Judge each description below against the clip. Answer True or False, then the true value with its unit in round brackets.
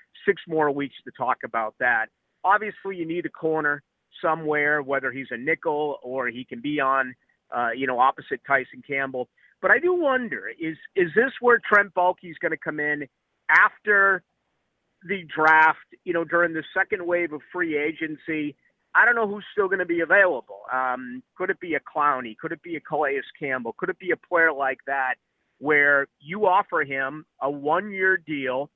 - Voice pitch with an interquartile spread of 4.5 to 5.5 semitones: True (4.8 semitones)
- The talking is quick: False (190 wpm)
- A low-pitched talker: False (155 Hz)